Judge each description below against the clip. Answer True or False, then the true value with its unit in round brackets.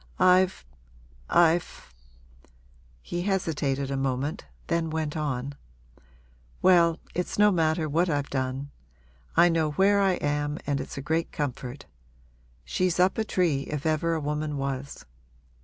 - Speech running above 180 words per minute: False (140 wpm)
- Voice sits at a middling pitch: True (155 Hz)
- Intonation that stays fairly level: False (3.8 semitones)